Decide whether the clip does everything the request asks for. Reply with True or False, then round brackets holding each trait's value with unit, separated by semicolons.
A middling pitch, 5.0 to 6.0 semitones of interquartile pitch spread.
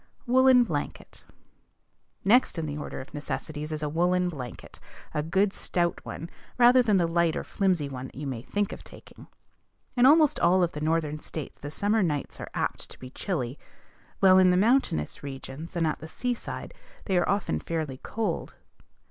True (170 Hz; 5.3 semitones)